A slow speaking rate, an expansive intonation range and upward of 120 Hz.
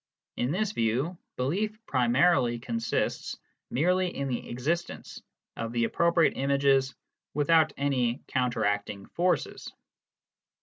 Yes: slow, 100 wpm; wide, 5.9 semitones; low, 135 Hz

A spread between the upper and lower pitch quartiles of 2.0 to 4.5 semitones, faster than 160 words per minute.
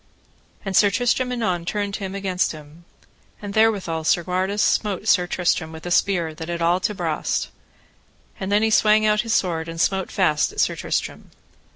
Yes: average, 3.6 semitones; average, 180 wpm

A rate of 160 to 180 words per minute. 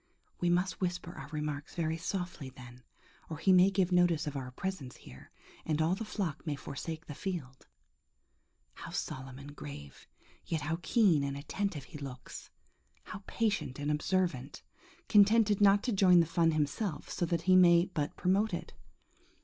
Yes: average, 165 wpm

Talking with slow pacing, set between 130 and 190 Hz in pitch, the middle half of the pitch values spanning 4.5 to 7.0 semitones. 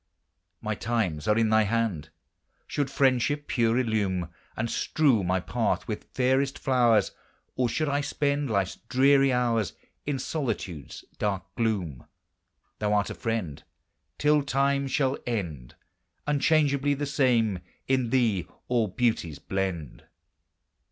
No: slow, 125 wpm; low, 115 Hz; wide, 5.5 semitones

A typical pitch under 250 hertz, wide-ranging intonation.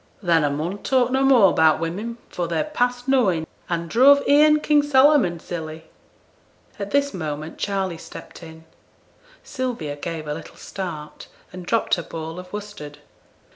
Yes: medium, 185 Hz; wide, 7.7 semitones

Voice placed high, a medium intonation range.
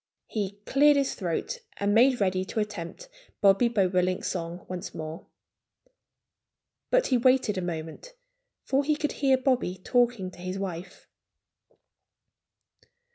No: high, 200 Hz; wide, 6.1 semitones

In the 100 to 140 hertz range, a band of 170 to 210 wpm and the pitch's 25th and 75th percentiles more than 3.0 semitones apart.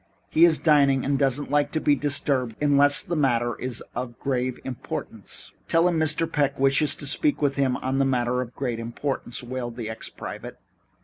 No: low, 135 Hz; average, 195 wpm; average, 2.7 semitones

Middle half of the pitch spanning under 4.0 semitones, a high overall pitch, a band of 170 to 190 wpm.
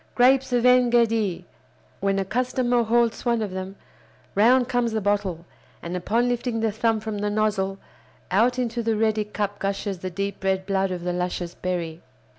Yes: average, 3.6 semitones; high, 210 Hz; average, 180 wpm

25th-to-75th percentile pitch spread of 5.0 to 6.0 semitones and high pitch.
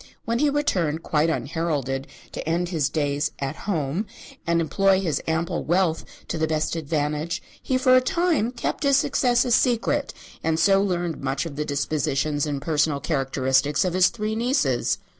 No: wide, 5.5 semitones; medium, 165 Hz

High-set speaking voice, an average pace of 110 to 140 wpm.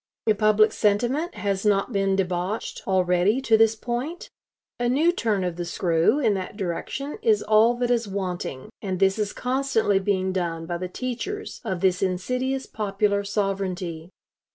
No: high, 200 Hz; average, 160 wpm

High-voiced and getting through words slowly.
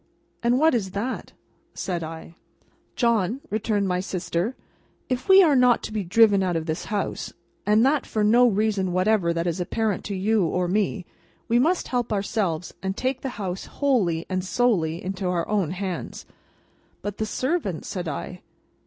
No: high, 200 Hz; average, 170 wpm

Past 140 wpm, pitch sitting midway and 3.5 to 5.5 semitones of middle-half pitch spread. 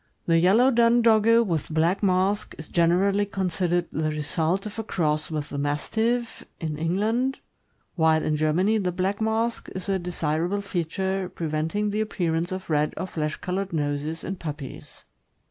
Yes: average, 160 wpm; medium, 180 Hz; average, 4.4 semitones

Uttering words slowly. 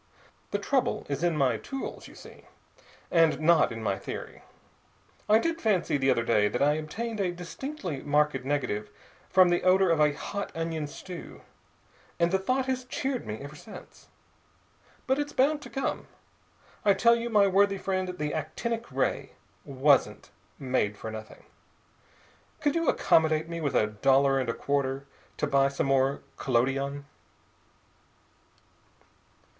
No: average, 150 wpm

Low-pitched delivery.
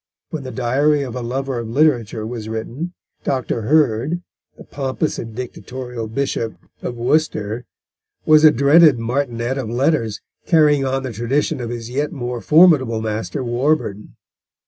Yes: low, 130 Hz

